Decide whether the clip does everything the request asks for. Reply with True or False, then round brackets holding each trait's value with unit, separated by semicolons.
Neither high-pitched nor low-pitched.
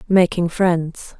True (175 Hz)